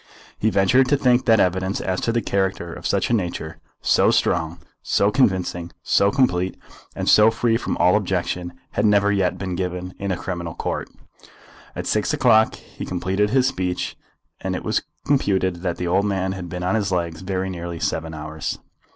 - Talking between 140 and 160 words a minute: No, average, 185 wpm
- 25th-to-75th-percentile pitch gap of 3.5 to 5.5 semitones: No, average, 2.8 semitones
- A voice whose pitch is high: No, very low, 95 Hz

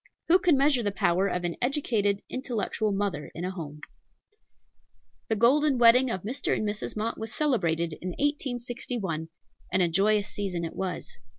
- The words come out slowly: No, average, 165 wpm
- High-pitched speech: Yes, high, 210 Hz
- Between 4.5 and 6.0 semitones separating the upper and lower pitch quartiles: Yes, average, 5.3 semitones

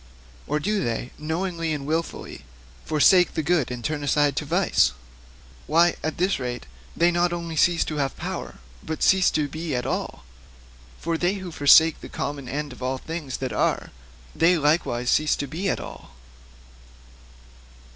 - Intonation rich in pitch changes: No, average, 3.4 semitones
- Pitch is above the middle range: No, medium, 155 Hz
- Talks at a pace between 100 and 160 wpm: No, average, 170 wpm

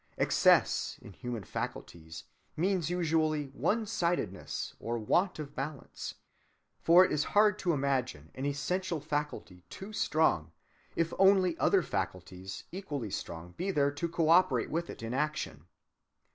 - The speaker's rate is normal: No, slow, 130 wpm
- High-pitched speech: No, medium, 150 Hz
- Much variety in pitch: Yes, wide, 7.2 semitones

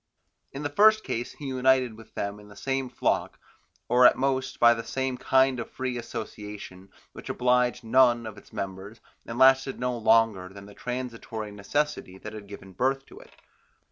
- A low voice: Yes, low, 120 Hz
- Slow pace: No, average, 175 wpm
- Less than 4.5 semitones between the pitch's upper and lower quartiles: Yes, average, 3.9 semitones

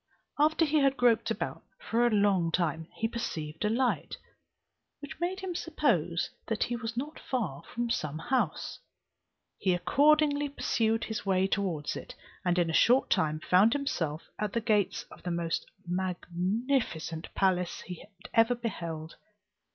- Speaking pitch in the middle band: No, high, 210 Hz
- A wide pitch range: Yes, wide, 6.8 semitones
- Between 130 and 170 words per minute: Yes, average, 150 wpm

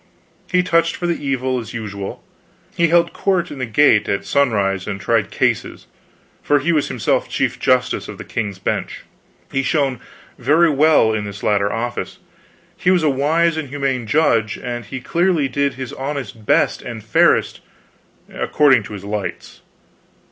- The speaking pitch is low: Yes, low, 130 Hz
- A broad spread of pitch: Yes, wide, 6.0 semitones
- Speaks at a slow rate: No, average, 165 wpm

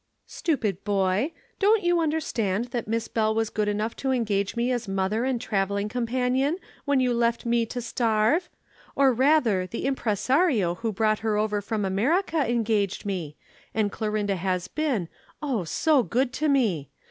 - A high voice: Yes, high, 225 Hz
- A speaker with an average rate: Yes, average, 160 wpm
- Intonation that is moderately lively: Yes, average, 4.3 semitones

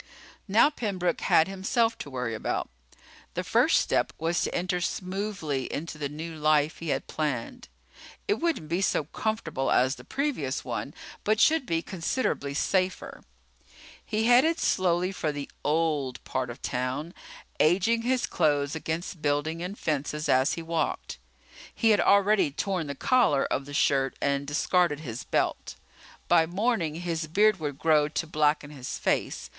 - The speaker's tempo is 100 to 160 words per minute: Yes, average, 155 wpm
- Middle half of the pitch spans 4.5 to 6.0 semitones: Yes, average, 5.1 semitones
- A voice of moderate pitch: Yes, medium, 165 Hz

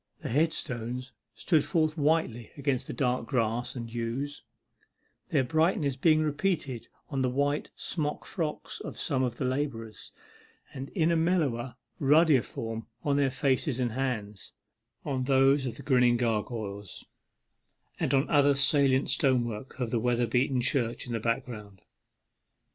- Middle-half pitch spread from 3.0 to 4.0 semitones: Yes, average, 3.4 semitones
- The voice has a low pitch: Yes, low, 130 Hz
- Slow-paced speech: No, average, 145 wpm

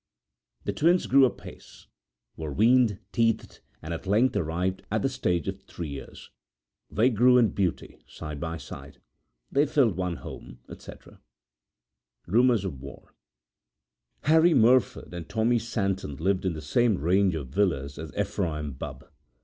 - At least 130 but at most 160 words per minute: Yes, average, 145 wpm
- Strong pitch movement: Yes, wide, 6.7 semitones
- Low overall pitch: Yes, very low, 95 Hz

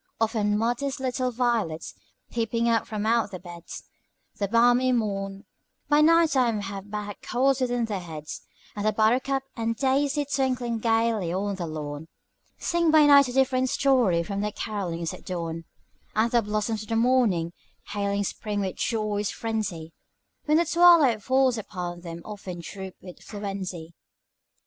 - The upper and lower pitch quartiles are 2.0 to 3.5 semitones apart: No, average, 4.5 semitones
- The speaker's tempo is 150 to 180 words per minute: Yes, average, 160 wpm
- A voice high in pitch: Yes, high, 220 Hz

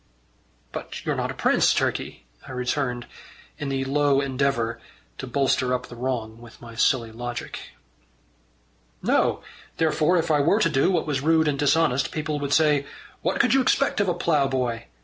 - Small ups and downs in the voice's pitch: No, average, 3.5 semitones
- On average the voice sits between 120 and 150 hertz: Yes, medium, 140 Hz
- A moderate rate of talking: Yes, average, 170 wpm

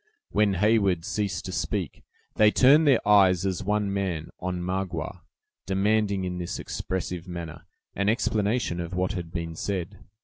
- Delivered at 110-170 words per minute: Yes, average, 150 wpm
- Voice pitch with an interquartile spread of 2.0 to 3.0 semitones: Yes, average, 2.7 semitones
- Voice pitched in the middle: No, very low, 95 Hz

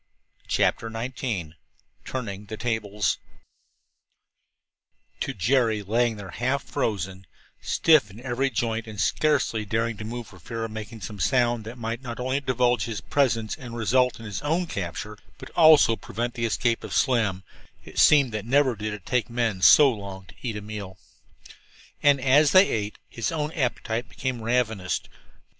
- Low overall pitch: Yes, low, 115 Hz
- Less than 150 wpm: No, average, 160 wpm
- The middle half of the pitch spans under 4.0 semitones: Yes, average, 3.3 semitones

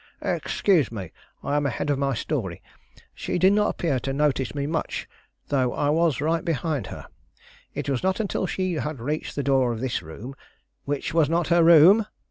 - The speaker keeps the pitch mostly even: No, average, 4.0 semitones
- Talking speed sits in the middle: Yes, average, 190 wpm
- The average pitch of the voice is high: No, medium, 145 Hz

